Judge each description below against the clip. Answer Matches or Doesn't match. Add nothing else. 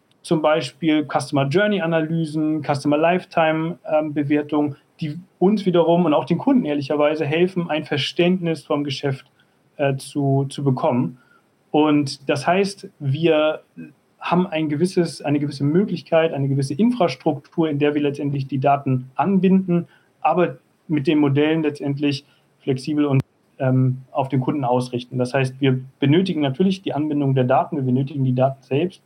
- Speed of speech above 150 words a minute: Doesn't match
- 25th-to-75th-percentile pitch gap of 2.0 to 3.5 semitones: Matches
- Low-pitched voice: Doesn't match